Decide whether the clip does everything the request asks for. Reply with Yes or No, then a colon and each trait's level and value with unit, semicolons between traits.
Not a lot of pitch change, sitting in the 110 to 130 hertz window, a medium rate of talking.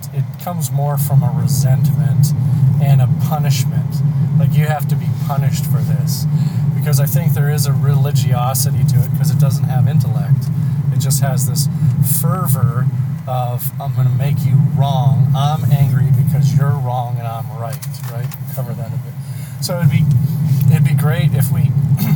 No: narrow, 1.1 semitones; medium, 140 Hz; average, 175 wpm